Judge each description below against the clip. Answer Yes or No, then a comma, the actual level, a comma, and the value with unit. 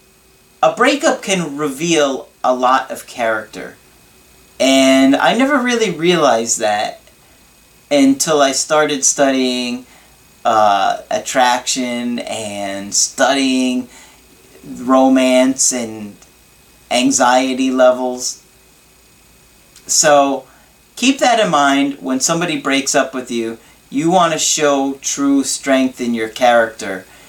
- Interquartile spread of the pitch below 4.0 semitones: Yes, average, 3.6 semitones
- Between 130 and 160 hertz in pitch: Yes, low, 135 Hz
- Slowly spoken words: Yes, slow, 100 wpm